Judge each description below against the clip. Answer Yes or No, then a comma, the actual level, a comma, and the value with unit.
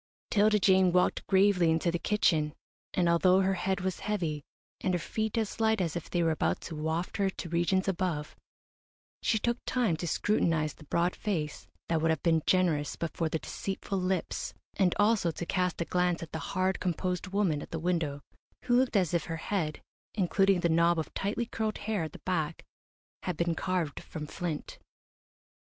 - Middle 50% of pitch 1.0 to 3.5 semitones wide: Yes, average, 3.0 semitones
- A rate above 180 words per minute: Yes, average, 190 wpm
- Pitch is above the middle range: No, medium, 180 Hz